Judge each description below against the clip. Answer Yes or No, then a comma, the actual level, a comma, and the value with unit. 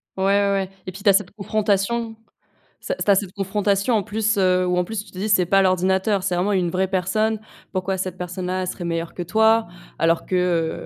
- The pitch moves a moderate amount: No, narrow, 2.3 semitones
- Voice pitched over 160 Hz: Yes, high, 190 Hz